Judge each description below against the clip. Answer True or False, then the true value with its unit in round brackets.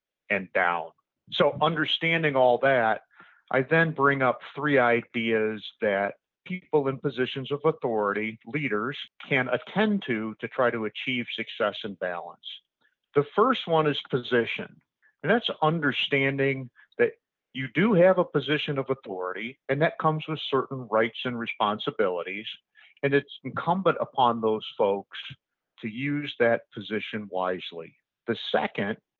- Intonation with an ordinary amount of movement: True (4.7 semitones)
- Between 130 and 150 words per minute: True (135 wpm)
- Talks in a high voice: False (135 Hz)